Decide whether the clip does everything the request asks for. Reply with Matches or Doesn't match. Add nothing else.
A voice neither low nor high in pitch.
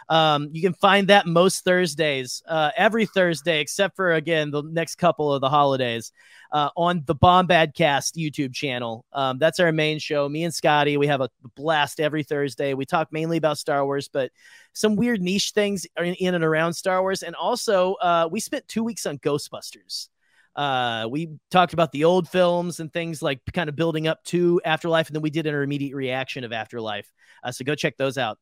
Matches